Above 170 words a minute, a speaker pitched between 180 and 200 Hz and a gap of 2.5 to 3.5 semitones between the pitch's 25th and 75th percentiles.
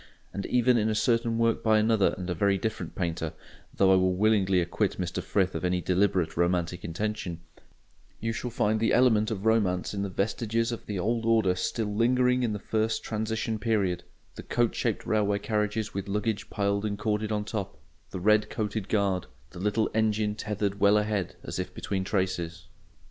No: average, 180 wpm; low, 105 Hz; average, 2.8 semitones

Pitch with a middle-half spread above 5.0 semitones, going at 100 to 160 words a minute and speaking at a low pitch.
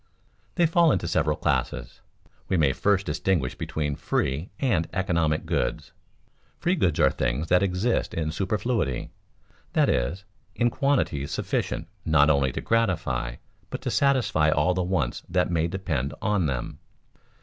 Yes: wide, 5.5 semitones; average, 150 wpm; very low, 85 Hz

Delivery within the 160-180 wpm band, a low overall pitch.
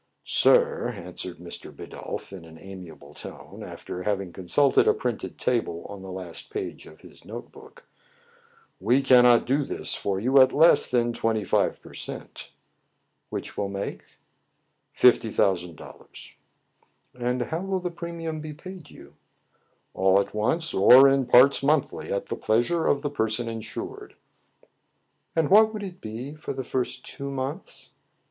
Yes: average, 175 wpm; low, 125 Hz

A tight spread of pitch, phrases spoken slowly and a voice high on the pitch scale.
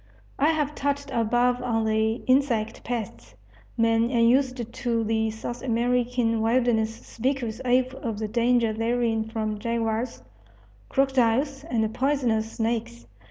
Yes: narrow, 2.1 semitones; slow, 125 wpm; high, 235 Hz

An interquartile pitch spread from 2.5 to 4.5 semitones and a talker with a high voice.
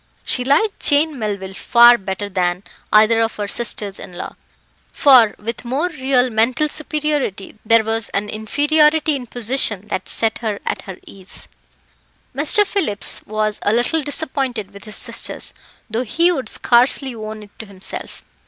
No: average, 4.9 semitones; high, 230 Hz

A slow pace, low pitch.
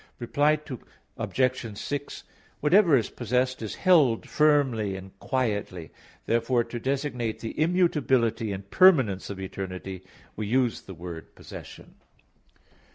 Yes: slow, 115 wpm; low, 120 Hz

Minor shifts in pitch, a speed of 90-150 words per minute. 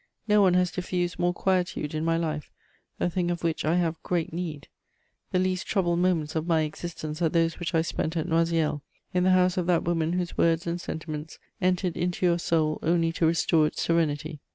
No: narrow, 1.9 semitones; fast, 205 wpm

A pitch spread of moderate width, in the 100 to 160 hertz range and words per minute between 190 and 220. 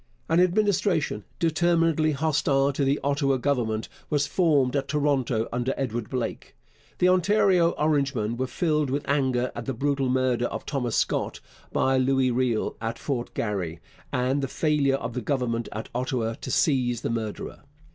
No: average, 3.6 semitones; low, 135 Hz; average, 155 wpm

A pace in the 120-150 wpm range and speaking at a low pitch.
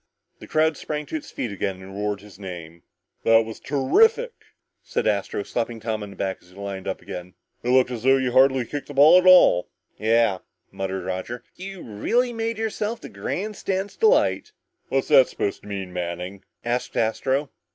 No: average, 185 wpm; low, 120 Hz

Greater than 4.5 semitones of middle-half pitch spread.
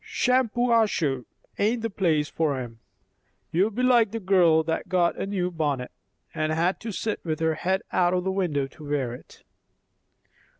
Yes: average, 5.0 semitones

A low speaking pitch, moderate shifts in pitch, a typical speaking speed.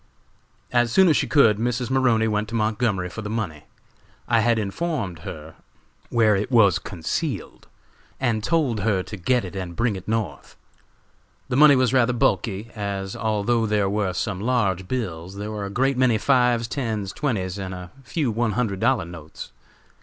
Yes: low, 110 Hz; average, 4.0 semitones; average, 175 wpm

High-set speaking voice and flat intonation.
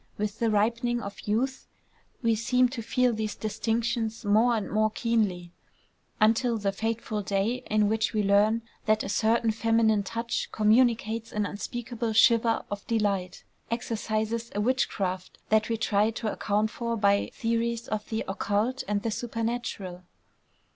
Yes: high, 220 Hz; narrow, 1.9 semitones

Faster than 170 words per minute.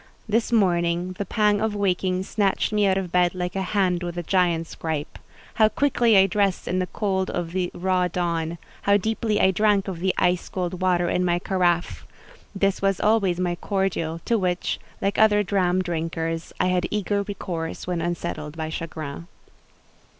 Yes: average, 180 wpm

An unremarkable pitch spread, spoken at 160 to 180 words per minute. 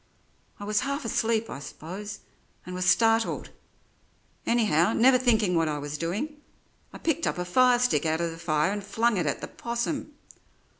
No: wide, 6.0 semitones; average, 170 wpm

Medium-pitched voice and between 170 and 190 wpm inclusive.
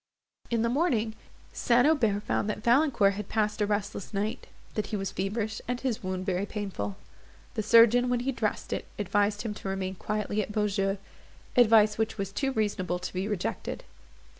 No: high, 210 Hz; average, 180 wpm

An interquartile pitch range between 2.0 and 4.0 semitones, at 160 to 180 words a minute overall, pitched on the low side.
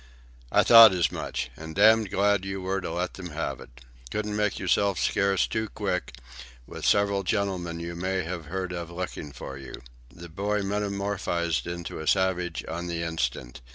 Yes: average, 2.8 semitones; average, 175 wpm; very low, 95 Hz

